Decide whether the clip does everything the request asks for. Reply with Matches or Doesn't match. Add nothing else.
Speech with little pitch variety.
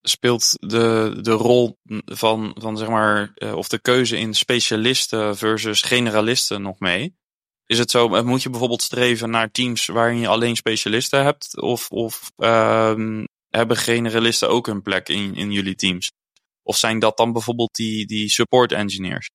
Matches